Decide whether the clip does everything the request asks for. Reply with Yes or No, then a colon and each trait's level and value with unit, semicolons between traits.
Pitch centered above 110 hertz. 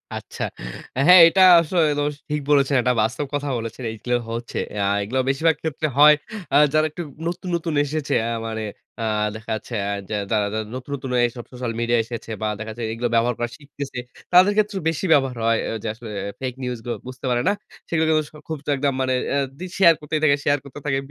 Yes: low, 135 Hz